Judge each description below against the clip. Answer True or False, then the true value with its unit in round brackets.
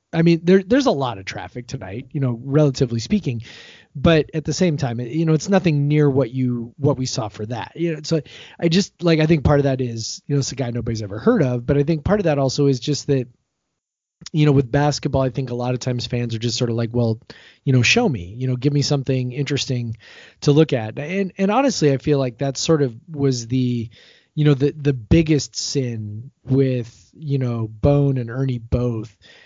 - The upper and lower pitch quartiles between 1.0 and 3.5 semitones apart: False (3.9 semitones)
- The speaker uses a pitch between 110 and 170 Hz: True (135 Hz)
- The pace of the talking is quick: True (235 wpm)